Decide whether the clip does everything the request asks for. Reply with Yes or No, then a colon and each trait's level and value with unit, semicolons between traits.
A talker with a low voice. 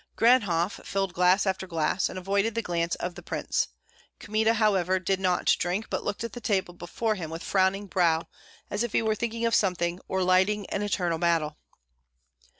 No: high, 190 Hz